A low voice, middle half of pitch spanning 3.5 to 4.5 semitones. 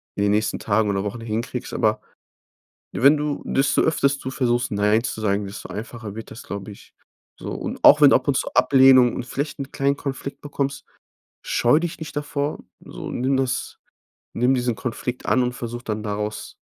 Yes: low, 125 Hz; average, 4.2 semitones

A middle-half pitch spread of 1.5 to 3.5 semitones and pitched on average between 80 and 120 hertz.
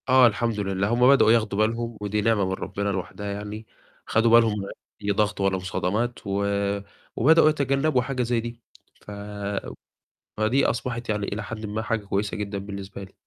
Yes: average, 2.8 semitones; low, 110 Hz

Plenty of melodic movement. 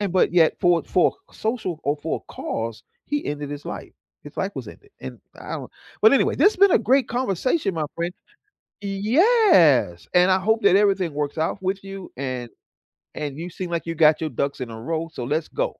Yes: wide, 6.0 semitones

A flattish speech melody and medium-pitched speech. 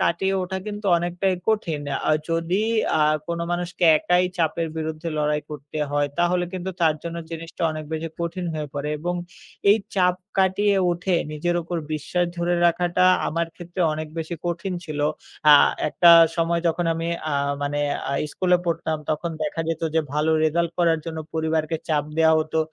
Yes: narrow, 2.0 semitones; medium, 170 Hz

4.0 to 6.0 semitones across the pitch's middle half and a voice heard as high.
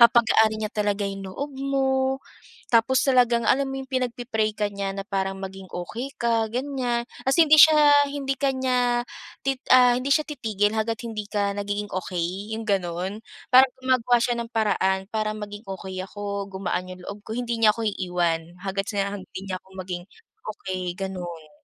Yes: average, 4.6 semitones; high, 215 Hz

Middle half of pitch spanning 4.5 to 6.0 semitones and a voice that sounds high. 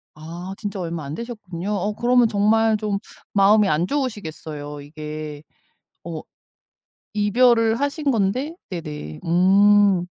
Yes: average, 5.3 semitones; high, 200 Hz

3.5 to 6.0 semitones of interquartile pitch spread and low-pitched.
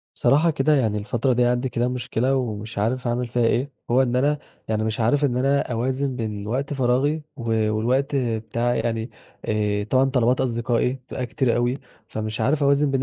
No: average, 2.9 semitones; low, 125 Hz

